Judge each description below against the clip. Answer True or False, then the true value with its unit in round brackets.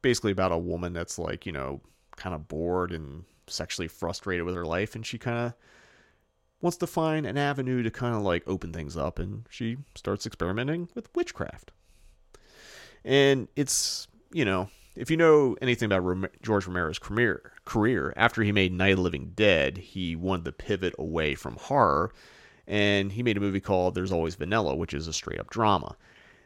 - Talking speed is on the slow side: False (185 wpm)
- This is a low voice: True (95 Hz)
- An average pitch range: False (5.9 semitones)